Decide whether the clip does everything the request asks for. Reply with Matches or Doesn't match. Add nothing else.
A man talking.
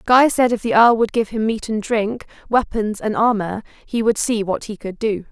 Doesn't match